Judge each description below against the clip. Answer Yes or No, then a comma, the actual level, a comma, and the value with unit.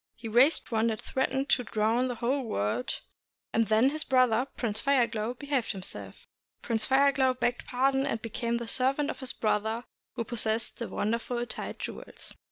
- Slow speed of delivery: No, average, 175 wpm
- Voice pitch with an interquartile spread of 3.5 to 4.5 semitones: No, average, 2.8 semitones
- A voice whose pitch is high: Yes, high, 240 Hz